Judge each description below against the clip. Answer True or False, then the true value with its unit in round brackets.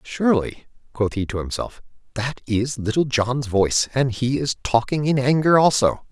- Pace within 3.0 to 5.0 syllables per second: True (4.8 syllables/s)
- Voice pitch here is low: True (125 Hz)